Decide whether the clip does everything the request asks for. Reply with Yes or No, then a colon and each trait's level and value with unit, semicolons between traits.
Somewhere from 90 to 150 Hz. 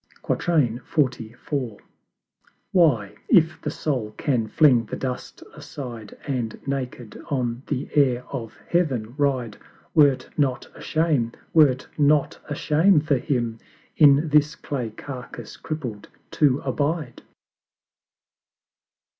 Yes: low, 135 Hz